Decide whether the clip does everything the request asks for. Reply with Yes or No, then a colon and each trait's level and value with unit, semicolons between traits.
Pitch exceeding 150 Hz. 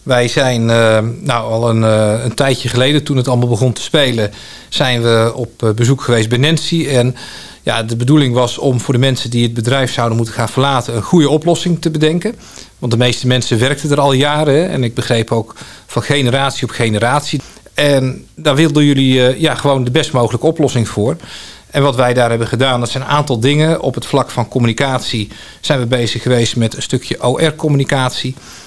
No: low, 130 Hz